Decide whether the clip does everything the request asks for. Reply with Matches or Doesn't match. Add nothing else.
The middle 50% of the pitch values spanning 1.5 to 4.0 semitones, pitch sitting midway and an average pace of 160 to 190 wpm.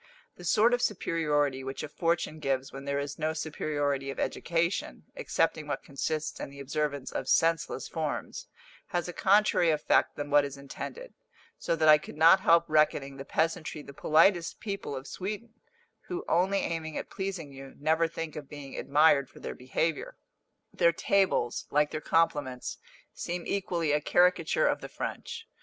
Matches